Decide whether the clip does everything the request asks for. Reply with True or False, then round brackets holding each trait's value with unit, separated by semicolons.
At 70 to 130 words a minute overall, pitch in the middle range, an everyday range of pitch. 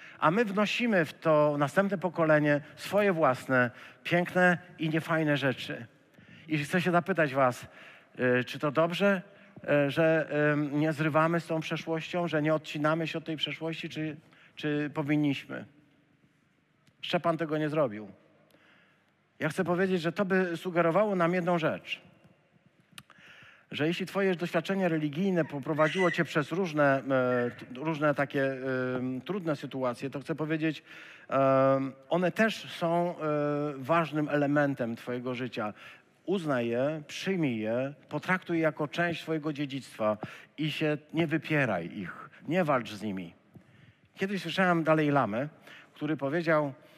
True (125 wpm; 155 Hz; 3.2 semitones)